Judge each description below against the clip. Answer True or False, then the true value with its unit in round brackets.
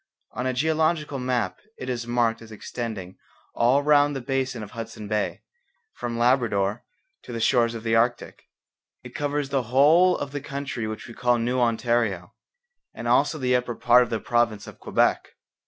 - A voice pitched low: True (120 Hz)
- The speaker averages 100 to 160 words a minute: False (175 wpm)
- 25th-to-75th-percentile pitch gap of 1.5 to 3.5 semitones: True (2.9 semitones)